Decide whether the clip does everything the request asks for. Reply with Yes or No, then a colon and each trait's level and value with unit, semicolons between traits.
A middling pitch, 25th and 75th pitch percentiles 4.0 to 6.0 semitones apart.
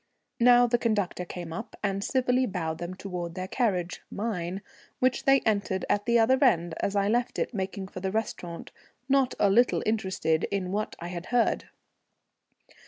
No: high, 200 Hz; average, 4.6 semitones